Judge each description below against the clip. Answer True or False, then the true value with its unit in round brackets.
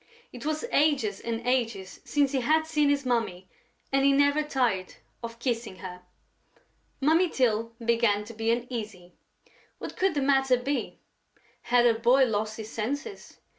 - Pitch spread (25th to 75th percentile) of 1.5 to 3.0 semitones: False (4.1 semitones)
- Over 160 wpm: False (155 wpm)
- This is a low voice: False (245 Hz)